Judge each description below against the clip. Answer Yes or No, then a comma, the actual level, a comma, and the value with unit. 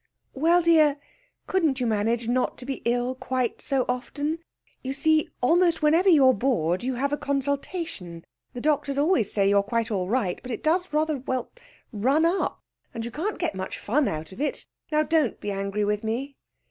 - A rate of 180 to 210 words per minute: Yes, average, 185 wpm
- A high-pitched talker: Yes, very high, 260 Hz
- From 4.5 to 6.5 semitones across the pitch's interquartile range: Yes, average, 5.2 semitones